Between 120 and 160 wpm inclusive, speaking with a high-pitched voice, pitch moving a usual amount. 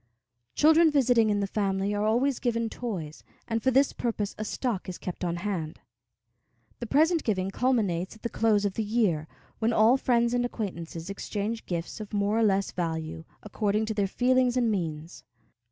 No: average, 180 wpm; high, 215 Hz; average, 4.0 semitones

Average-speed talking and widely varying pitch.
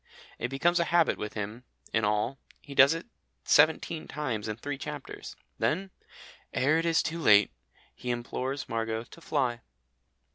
Yes: average, 155 wpm; wide, 5.8 semitones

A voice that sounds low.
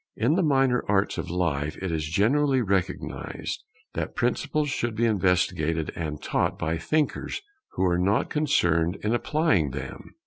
Yes: very low, 95 Hz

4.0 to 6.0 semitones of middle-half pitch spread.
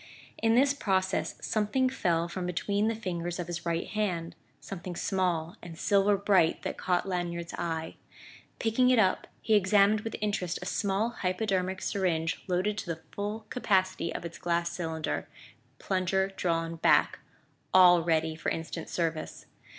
No: average, 3.2 semitones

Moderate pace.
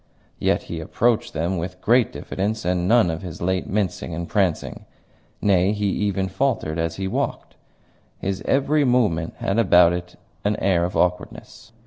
Yes: average, 160 wpm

